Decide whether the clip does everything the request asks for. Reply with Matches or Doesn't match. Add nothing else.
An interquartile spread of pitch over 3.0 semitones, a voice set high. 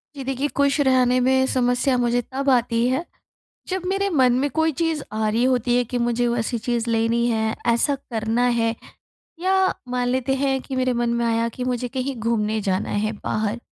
Doesn't match